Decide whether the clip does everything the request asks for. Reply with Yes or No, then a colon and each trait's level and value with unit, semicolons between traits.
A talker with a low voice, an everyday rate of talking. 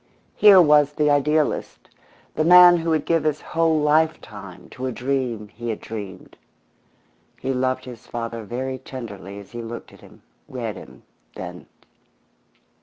Yes: low, 130 Hz; average, 150 wpm